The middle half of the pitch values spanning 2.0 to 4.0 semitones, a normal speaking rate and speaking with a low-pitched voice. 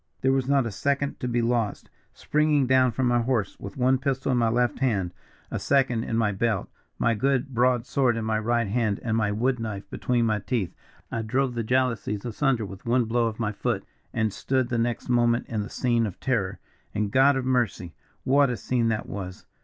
No: average, 3.0 semitones; fast, 215 wpm; low, 120 Hz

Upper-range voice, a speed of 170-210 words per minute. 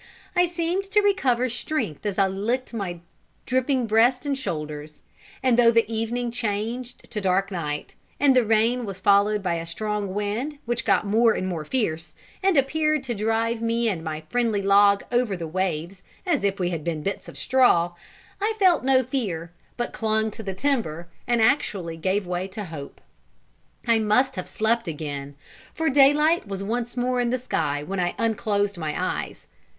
Yes: high, 220 Hz; average, 175 wpm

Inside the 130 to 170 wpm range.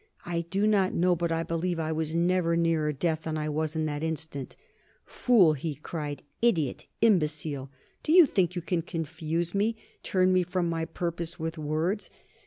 No: average, 180 wpm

